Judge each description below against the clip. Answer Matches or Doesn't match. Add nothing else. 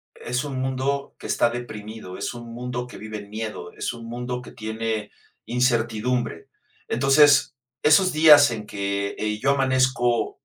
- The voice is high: Doesn't match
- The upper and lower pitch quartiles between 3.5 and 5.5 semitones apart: Doesn't match